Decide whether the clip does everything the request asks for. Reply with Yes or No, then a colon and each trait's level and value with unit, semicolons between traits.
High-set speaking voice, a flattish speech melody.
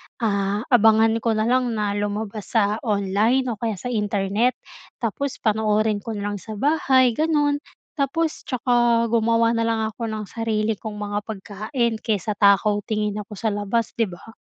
Yes: high, 220 Hz; narrow, 2.2 semitones